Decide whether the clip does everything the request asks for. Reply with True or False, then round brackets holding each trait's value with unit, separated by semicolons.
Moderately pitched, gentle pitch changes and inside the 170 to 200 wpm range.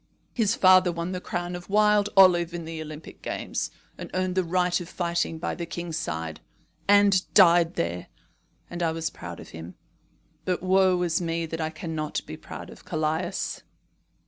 True (175 Hz; 2.2 semitones; 175 wpm)